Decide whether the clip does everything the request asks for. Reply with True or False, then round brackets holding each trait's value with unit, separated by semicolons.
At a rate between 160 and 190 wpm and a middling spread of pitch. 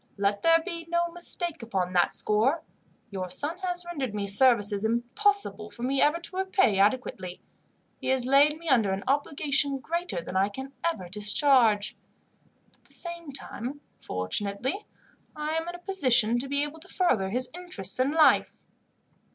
False (165 wpm; 8.2 semitones)